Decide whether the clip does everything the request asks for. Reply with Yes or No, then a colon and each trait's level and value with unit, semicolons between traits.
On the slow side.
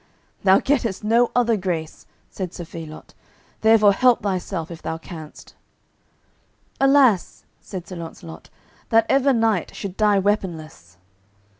Yes: slow, 125 wpm